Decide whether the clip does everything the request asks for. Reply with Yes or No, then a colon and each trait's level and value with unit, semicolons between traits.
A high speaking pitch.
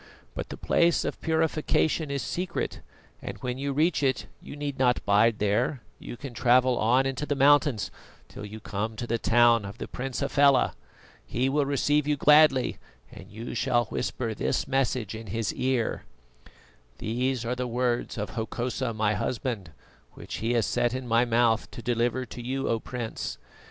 No: low, 125 Hz